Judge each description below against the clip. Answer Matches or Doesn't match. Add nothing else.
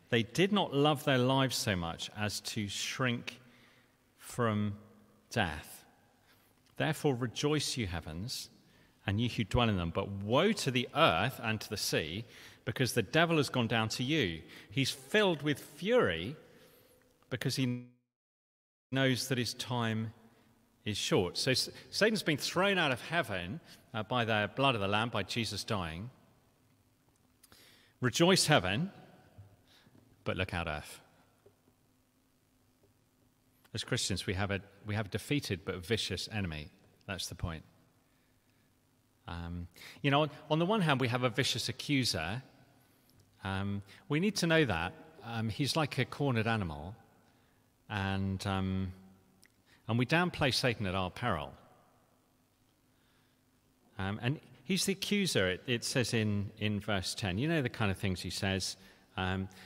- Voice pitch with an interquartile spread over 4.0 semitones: Matches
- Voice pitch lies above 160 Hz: Doesn't match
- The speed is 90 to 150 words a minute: Matches